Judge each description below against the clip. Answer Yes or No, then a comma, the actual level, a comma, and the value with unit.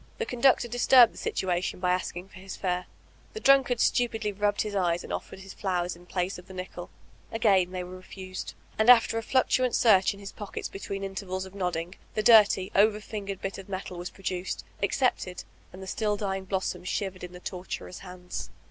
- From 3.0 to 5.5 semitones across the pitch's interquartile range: No, narrow, 2.6 semitones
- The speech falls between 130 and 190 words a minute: No, fast, 205 wpm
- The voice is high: Yes, high, 195 Hz